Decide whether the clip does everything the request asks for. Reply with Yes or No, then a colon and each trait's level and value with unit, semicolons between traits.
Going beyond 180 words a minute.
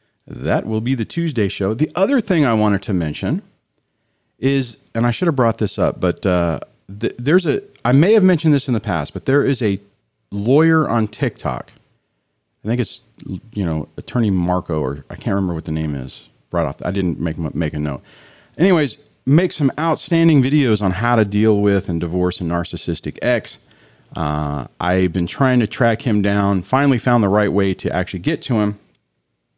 Yes: average, 195 wpm